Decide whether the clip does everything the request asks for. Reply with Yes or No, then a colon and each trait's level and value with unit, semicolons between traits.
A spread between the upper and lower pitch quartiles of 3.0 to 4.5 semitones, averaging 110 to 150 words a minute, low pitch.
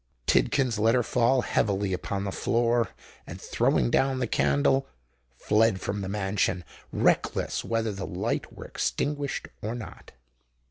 Yes: average, 3.8 semitones; average, 140 wpm; low, 110 Hz